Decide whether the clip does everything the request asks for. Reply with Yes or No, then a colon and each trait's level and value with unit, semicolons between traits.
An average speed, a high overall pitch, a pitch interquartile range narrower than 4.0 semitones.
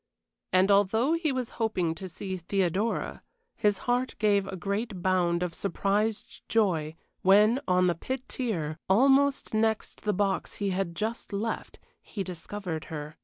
Yes: average, 150 wpm; high, 200 Hz; average, 3.5 semitones